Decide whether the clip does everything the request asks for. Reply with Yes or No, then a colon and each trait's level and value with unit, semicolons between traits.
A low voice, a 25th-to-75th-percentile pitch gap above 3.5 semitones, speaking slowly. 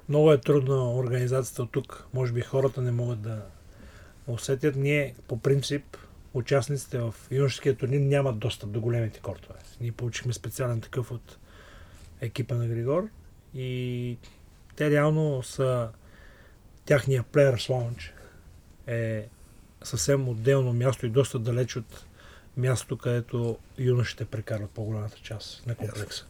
No: low, 120 Hz; average, 3.9 semitones; average, 130 wpm